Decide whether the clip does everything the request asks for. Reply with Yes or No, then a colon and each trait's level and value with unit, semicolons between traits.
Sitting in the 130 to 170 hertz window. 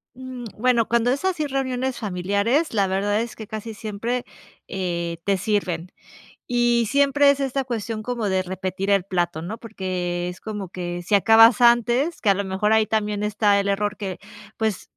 No: high, 210 Hz